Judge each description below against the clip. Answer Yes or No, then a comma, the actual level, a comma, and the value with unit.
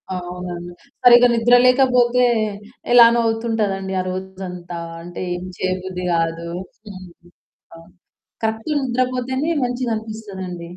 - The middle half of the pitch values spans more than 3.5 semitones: Yes, average, 5.1 semitones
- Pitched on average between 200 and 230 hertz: Yes, high, 205 Hz